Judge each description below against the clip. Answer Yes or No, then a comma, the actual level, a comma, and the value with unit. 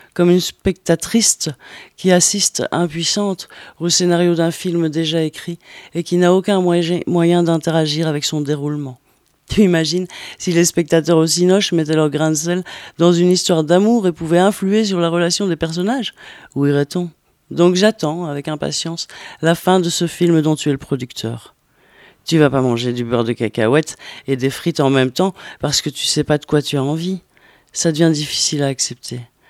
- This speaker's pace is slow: No, average, 185 wpm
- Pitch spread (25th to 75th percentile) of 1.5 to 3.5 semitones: Yes, average, 2.9 semitones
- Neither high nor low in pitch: Yes, medium, 165 Hz